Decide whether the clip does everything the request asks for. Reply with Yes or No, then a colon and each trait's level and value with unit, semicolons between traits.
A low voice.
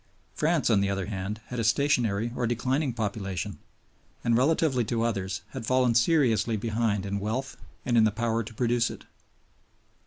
Yes: low, 115 Hz